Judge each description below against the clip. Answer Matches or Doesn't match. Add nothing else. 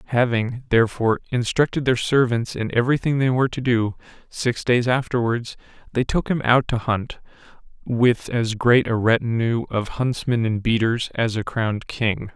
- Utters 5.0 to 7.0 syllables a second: Doesn't match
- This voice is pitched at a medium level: Doesn't match